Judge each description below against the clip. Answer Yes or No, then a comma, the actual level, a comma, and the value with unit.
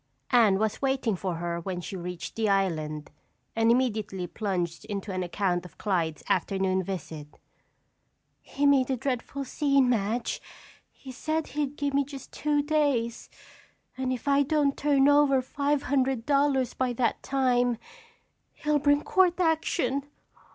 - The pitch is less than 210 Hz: No, very high, 250 Hz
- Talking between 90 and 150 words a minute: Yes, average, 145 wpm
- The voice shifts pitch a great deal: Yes, wide, 6.5 semitones